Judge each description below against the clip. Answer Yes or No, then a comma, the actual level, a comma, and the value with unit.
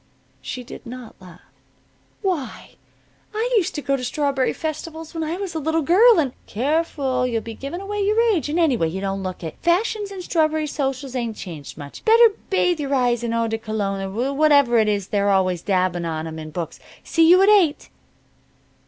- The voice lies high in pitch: Yes, very high, 270 Hz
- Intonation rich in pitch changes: Yes, wide, 8.2 semitones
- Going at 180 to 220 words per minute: Yes, average, 200 wpm